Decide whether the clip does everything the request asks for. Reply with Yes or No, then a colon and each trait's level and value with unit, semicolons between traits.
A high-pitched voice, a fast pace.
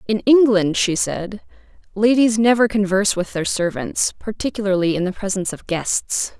No: high, 205 Hz; average, 150 wpm